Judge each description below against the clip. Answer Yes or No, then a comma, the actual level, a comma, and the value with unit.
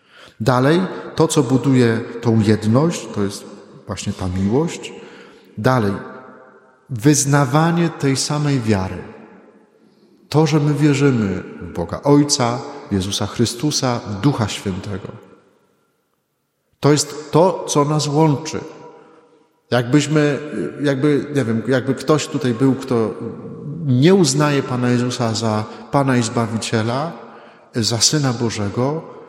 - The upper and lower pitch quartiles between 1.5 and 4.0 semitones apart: No, average, 4.7 semitones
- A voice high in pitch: No, low, 130 Hz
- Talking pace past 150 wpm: No, slow, 110 wpm